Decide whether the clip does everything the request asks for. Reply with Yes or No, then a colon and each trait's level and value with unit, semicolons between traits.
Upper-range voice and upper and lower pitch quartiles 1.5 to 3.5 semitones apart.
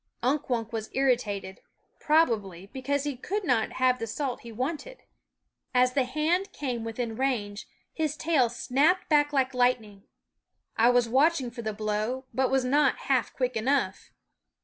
No: very high, 255 Hz; average, 3.9 semitones